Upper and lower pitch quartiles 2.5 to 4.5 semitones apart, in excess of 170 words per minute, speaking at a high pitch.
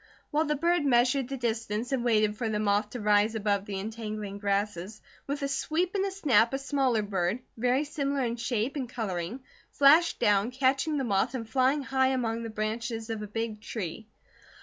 Yes: average, 4.2 semitones; average, 195 wpm; high, 230 Hz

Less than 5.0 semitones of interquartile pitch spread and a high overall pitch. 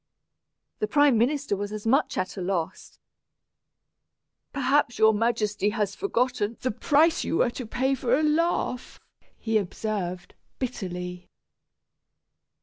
Yes: average, 4.6 semitones; high, 225 Hz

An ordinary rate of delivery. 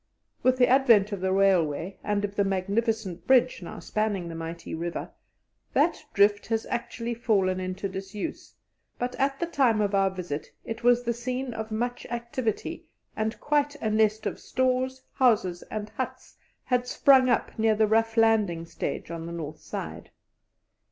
Yes: average, 165 wpm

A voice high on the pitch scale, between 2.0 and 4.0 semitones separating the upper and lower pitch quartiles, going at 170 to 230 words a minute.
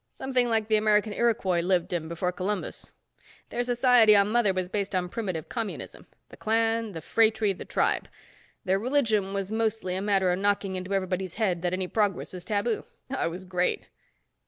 Yes: high, 200 Hz; average, 3.3 semitones; average, 180 wpm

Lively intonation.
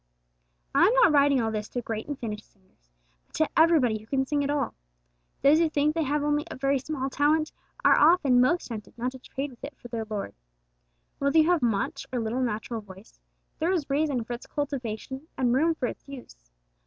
No: average, 4.4 semitones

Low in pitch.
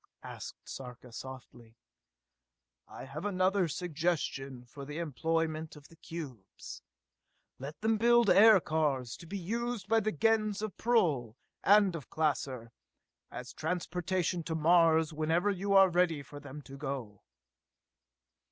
No: medium, 165 Hz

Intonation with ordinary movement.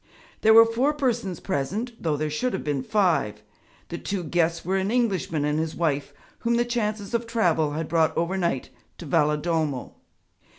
No: wide, 6.7 semitones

